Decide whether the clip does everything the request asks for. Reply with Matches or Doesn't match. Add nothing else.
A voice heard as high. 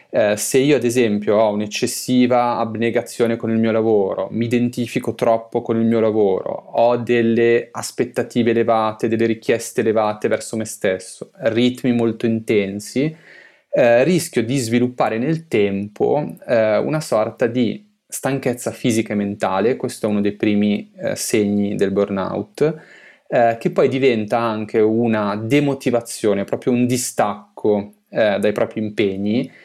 Doesn't match